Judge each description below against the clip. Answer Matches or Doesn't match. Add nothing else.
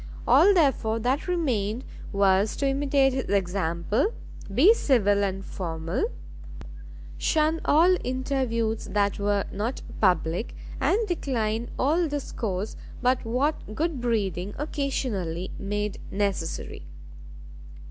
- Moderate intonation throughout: Doesn't match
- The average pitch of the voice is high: Matches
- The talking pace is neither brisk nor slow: Doesn't match